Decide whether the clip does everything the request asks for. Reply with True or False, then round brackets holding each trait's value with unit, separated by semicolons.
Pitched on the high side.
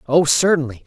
False (150 Hz)